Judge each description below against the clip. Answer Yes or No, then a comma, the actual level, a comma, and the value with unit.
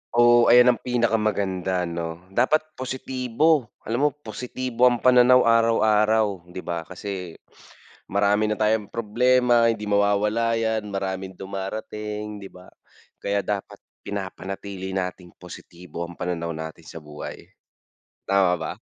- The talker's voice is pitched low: Yes, low, 105 Hz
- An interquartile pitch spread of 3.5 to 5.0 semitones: Yes, average, 3.8 semitones